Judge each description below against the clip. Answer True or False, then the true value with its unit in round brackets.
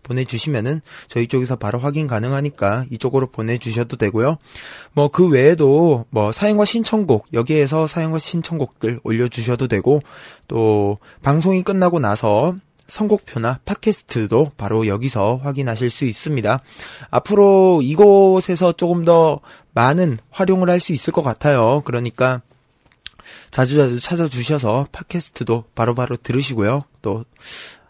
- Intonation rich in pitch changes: True (5.8 semitones)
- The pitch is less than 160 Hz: True (135 Hz)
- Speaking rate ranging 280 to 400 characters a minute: True (315 characters per minute)